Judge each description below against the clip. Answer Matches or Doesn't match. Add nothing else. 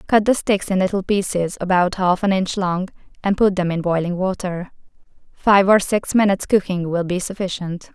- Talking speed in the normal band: Matches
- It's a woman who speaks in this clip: Matches